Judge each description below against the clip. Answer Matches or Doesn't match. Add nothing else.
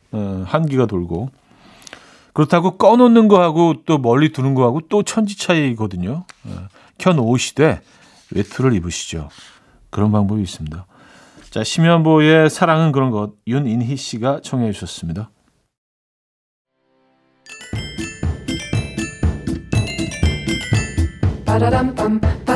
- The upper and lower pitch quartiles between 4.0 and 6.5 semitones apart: Doesn't match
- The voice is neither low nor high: Doesn't match